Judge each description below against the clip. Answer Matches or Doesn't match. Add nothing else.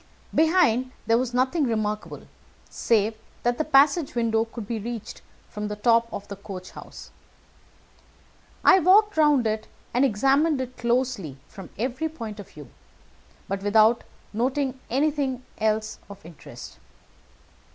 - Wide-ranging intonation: Doesn't match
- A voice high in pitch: Matches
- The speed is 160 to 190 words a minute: Doesn't match